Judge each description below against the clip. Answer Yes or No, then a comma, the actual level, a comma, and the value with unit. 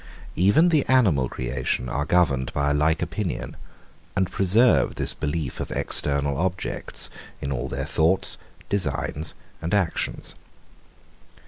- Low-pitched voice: Yes, very low, 80 Hz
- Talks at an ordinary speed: No, slow, 125 wpm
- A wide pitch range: No, average, 5.0 semitones